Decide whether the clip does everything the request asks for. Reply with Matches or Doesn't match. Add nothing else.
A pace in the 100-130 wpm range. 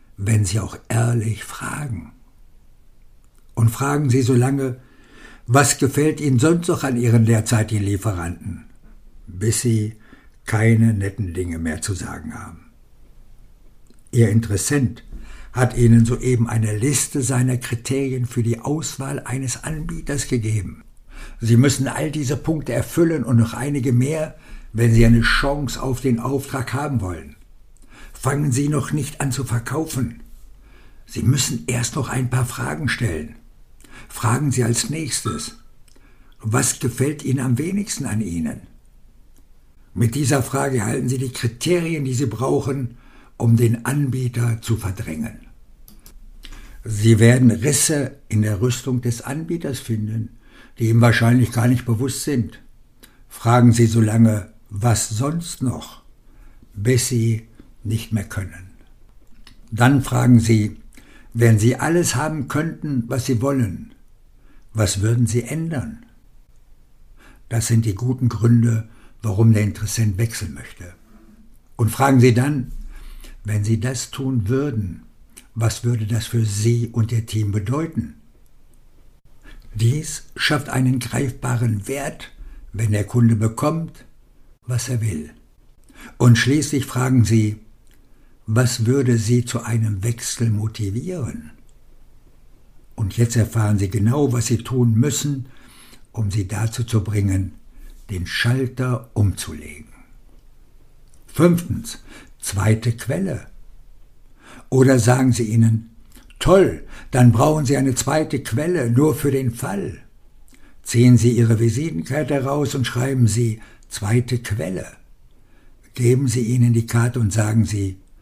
Matches